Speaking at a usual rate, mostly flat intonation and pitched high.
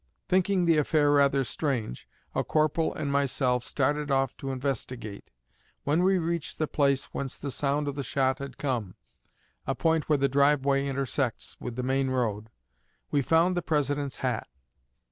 No: average, 165 wpm; narrow, 2.3 semitones; medium, 140 Hz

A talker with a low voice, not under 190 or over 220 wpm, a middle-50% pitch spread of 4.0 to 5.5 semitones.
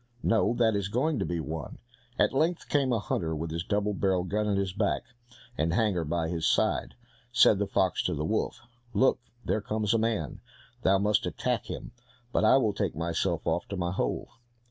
Yes: low, 100 Hz; average, 200 wpm; average, 4.3 semitones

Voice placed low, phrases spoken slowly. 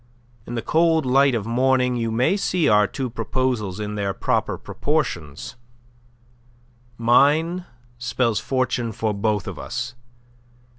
Yes: low, 120 Hz; slow, 130 wpm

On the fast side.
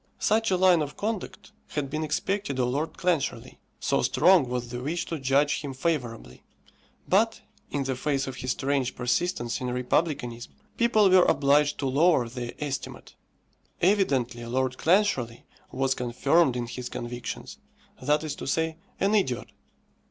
No: average, 150 wpm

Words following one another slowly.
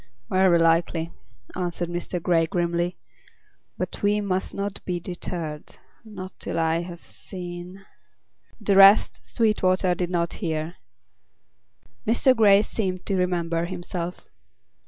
Yes: slow, 115 wpm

